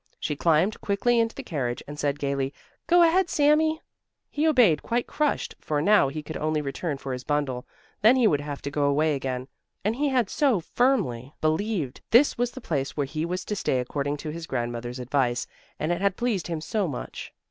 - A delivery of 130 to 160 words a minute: No, fast, 205 wpm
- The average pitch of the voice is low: No, medium, 155 Hz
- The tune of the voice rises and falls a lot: Yes, wide, 8.5 semitones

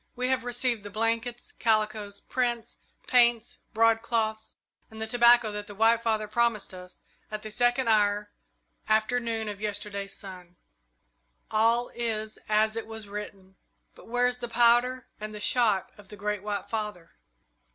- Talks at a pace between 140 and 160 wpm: Yes, average, 150 wpm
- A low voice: No, high, 220 Hz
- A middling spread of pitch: No, narrow, 2.3 semitones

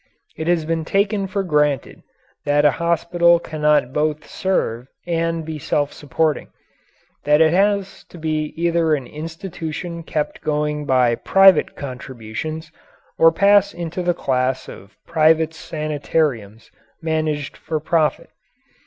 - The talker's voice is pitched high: No, medium, 155 Hz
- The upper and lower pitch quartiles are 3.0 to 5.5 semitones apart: No, narrow, 2.4 semitones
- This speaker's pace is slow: Yes, slow, 125 wpm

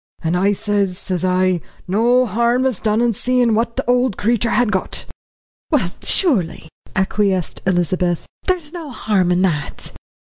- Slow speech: No, average, 155 wpm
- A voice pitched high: Yes, high, 210 Hz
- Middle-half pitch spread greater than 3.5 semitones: Yes, average, 4.8 semitones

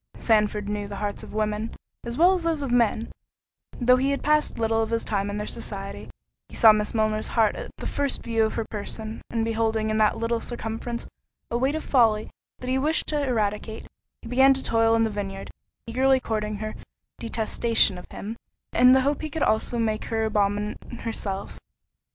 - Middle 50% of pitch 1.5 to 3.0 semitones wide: Yes, average, 2.7 semitones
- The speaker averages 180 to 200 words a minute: Yes, average, 195 wpm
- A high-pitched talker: Yes, high, 225 Hz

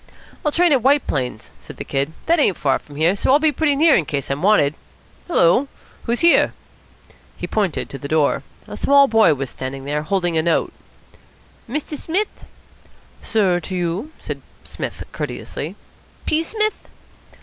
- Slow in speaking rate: No, average, 170 wpm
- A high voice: Yes, high, 195 Hz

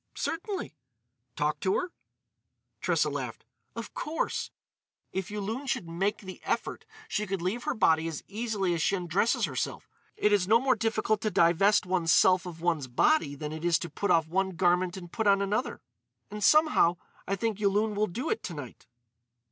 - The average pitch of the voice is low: No, high, 195 Hz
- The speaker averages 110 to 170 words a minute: No, average, 180 wpm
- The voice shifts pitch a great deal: No, average, 3.9 semitones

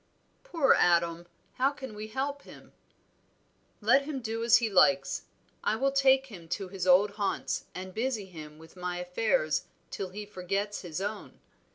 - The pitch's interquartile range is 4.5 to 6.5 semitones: Yes, wide, 5.5 semitones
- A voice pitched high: Yes, high, 205 Hz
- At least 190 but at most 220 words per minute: No, average, 165 wpm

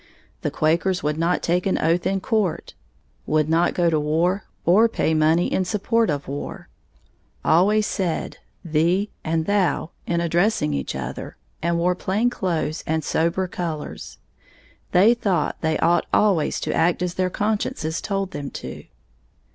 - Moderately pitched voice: Yes, medium, 175 Hz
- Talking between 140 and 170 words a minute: Yes, average, 155 wpm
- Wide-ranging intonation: No, average, 3.2 semitones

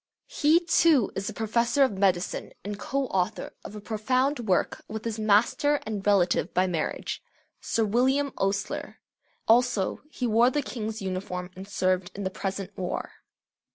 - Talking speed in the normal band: Yes, average, 155 wpm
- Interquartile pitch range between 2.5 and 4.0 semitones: No, average, 4.4 semitones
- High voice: Yes, high, 215 Hz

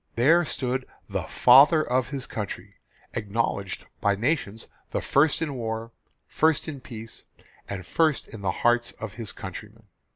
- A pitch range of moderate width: Yes, average, 4.4 semitones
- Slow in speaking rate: No, average, 150 wpm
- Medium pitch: No, low, 120 Hz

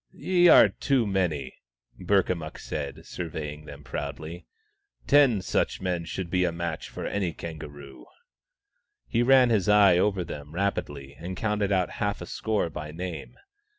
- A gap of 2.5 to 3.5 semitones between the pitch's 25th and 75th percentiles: No, average, 4.9 semitones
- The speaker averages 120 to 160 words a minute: Yes, average, 155 wpm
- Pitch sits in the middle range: No, very low, 90 Hz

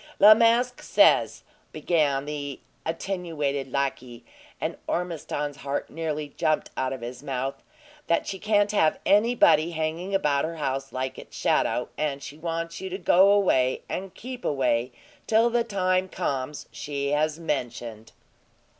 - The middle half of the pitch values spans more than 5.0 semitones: Yes, wide, 5.4 semitones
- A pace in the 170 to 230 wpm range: No, average, 145 wpm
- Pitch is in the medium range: Yes, medium, 155 Hz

